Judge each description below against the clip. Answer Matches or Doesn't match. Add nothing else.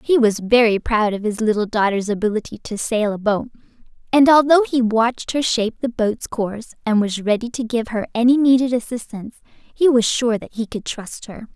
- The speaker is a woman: Matches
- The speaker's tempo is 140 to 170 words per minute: Doesn't match